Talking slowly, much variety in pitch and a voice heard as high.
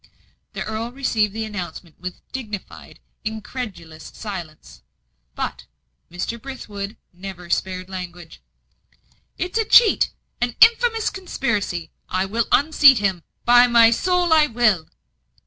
Yes: slow, 115 wpm; wide, 5.9 semitones; high, 220 Hz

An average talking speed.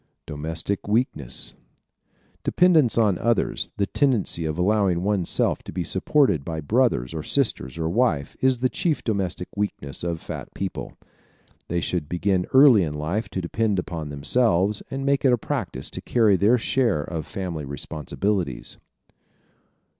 Yes: average, 155 wpm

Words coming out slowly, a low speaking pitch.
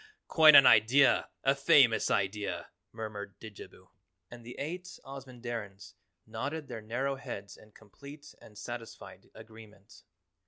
Yes: slow, 120 wpm; low, 115 Hz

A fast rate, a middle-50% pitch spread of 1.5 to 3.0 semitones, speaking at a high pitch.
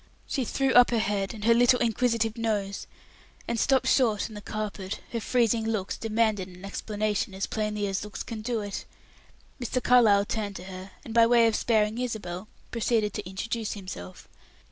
No: average, 180 wpm; narrow, 2.5 semitones; high, 215 Hz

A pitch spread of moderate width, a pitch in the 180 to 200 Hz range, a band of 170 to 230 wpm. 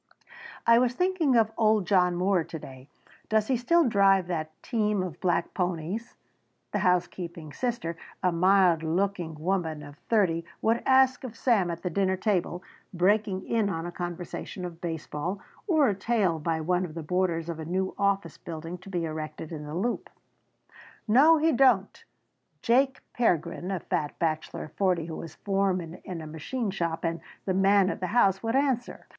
Yes: average, 4.5 semitones; medium, 185 Hz; average, 175 wpm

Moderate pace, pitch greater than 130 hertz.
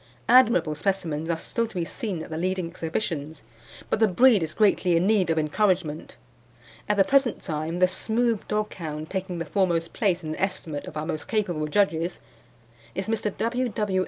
Yes: average, 190 wpm; medium, 185 Hz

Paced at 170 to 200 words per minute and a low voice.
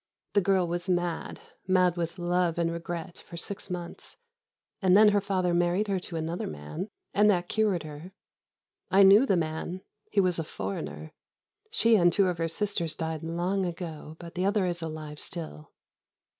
No: average, 175 wpm; medium, 175 Hz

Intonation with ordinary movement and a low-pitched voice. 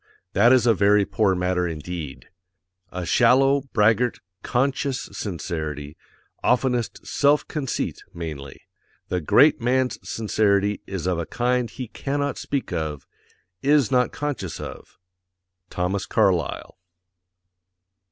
No: wide, 6.3 semitones; low, 105 Hz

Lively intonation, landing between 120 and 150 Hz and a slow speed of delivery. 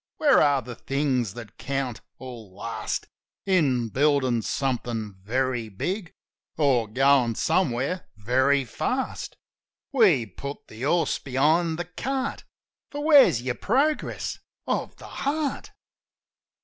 Yes: wide, 6.5 semitones; low, 135 Hz; slow, 115 wpm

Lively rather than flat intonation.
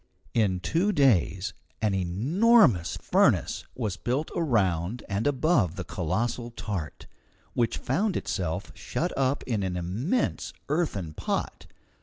Yes: wide, 7.5 semitones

